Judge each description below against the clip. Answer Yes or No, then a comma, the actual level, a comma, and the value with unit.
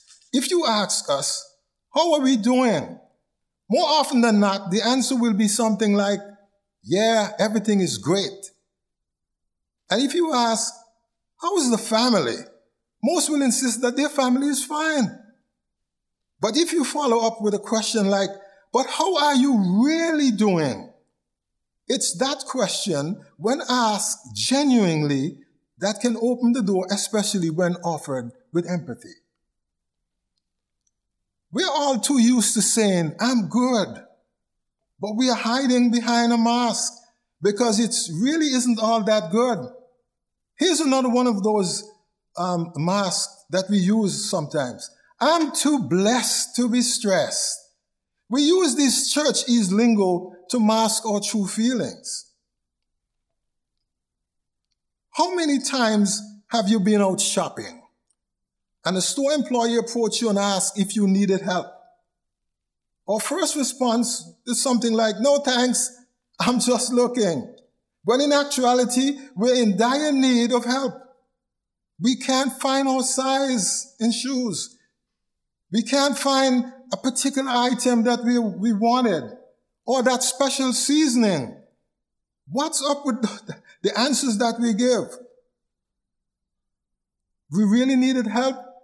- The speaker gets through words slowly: Yes, slow, 130 wpm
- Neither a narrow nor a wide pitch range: Yes, average, 4.4 semitones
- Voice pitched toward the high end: Yes, high, 235 Hz